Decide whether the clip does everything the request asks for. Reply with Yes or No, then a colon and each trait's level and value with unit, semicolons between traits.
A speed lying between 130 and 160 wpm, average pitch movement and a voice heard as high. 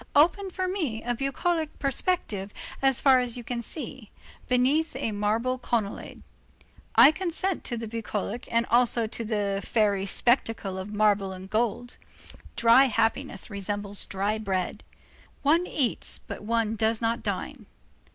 Yes: average, 140 wpm; average, 4.3 semitones; high, 230 Hz